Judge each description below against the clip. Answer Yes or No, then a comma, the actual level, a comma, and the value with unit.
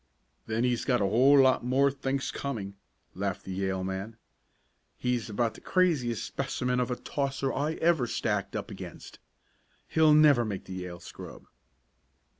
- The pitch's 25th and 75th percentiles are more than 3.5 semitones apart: Yes, average, 5.2 semitones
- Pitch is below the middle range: Yes, low, 125 Hz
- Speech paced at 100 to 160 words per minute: Yes, average, 155 wpm